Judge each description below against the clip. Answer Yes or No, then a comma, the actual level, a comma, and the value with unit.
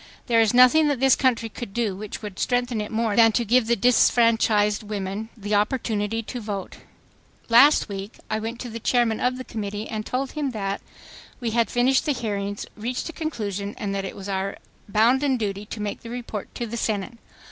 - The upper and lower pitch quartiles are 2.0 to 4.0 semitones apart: Yes, average, 2.9 semitones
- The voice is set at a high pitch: Yes, high, 225 Hz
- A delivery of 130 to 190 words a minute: No, average, 200 wpm